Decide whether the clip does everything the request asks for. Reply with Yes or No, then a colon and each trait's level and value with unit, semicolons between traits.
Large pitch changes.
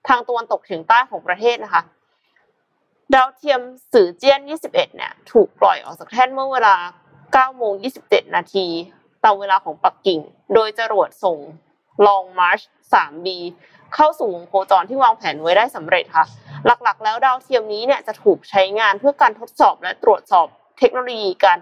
Yes: wide, 6.1 semitones